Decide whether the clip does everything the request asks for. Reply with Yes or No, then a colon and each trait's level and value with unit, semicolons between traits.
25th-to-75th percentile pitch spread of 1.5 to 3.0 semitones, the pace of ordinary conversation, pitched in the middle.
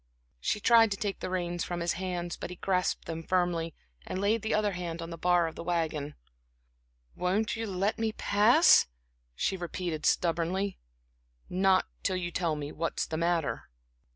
Yes: average, 2.7 semitones; average, 175 wpm; medium, 180 Hz